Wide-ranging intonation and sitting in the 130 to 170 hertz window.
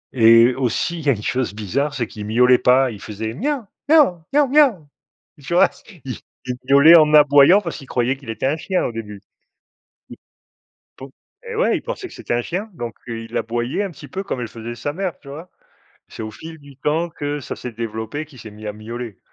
Yes: wide, 6.3 semitones; low, 135 Hz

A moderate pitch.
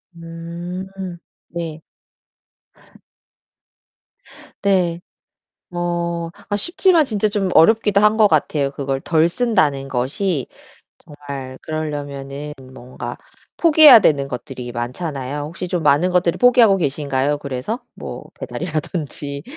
Yes: medium, 165 Hz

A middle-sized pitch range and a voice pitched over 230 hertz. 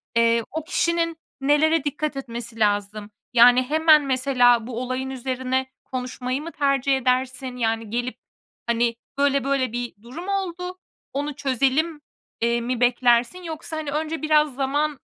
Yes: average, 3.8 semitones; very high, 265 Hz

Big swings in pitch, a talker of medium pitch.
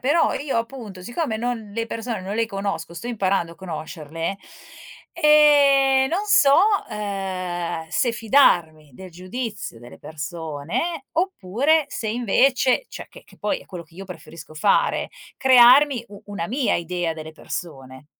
No: wide, 7.4 semitones; high, 205 Hz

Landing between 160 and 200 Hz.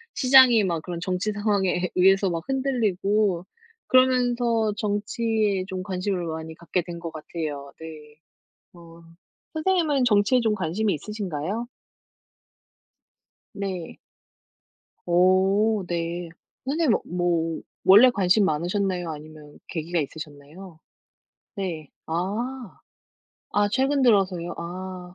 Yes: medium, 185 Hz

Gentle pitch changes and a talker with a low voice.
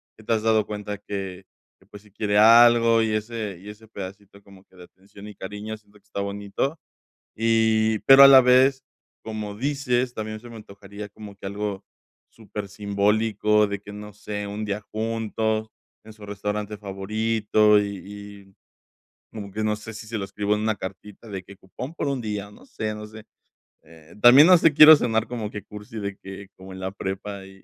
Yes: narrow, 1.8 semitones; low, 105 Hz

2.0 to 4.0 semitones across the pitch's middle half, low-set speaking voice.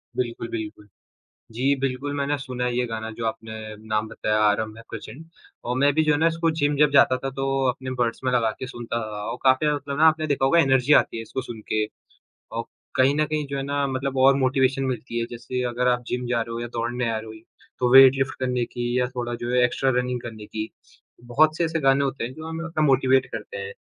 Yes: average, 3.0 semitones; low, 125 Hz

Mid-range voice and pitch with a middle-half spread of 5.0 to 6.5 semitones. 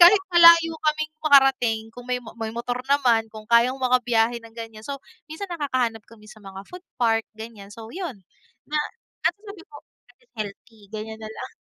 No: high, 245 Hz; wide, 5.5 semitones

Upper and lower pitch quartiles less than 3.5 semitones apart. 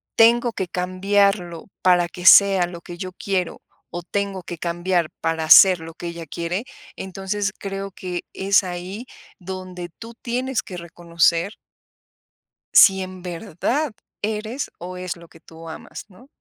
Yes: narrow, 2.5 semitones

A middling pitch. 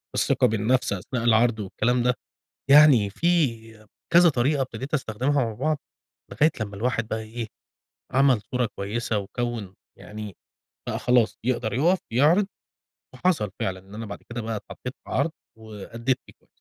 No: low, 120 Hz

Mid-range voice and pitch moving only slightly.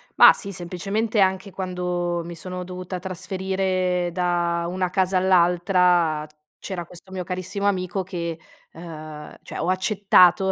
Yes: medium, 180 Hz; narrow, 1.4 semitones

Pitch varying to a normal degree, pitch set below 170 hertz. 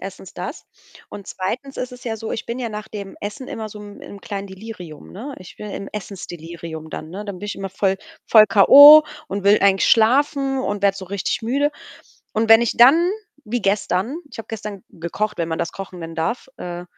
No: average, 3.2 semitones; high, 205 Hz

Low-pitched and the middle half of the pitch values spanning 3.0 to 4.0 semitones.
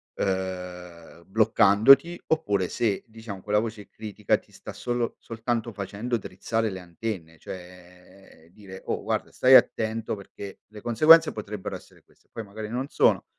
Yes: low, 105 Hz; average, 3.4 semitones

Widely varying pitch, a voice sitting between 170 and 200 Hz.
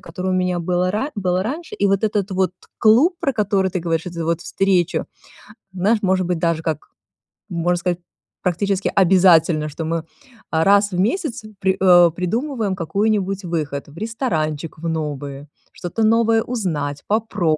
No: average, 3.8 semitones; medium, 185 Hz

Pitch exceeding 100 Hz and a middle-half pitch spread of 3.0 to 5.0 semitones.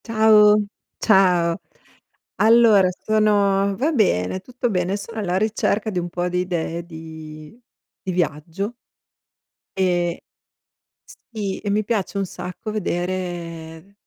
Yes: high, 190 Hz; average, 3.4 semitones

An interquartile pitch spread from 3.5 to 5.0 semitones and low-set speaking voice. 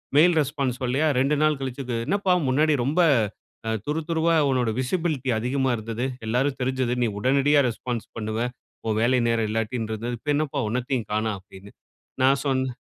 Yes: average, 3.8 semitones; low, 130 Hz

